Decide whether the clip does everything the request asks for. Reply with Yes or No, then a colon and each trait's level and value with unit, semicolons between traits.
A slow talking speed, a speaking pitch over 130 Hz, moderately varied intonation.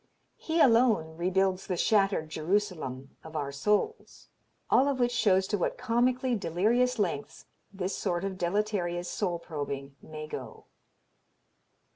No: slow, 130 wpm; high, 190 Hz; wide, 5.9 semitones